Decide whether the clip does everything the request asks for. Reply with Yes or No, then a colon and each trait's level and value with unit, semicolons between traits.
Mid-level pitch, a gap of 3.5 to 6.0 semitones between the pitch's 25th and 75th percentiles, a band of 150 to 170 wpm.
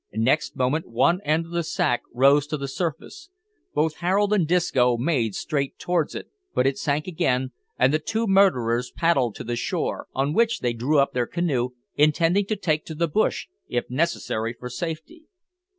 No: medium, 150 Hz; average, 5.3 semitones; average, 180 wpm